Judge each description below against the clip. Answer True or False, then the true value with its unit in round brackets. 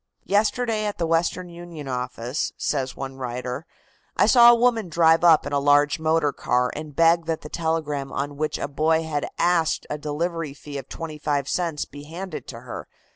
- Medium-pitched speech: True (155 Hz)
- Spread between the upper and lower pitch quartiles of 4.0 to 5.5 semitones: False (3.0 semitones)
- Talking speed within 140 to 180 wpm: False (190 wpm)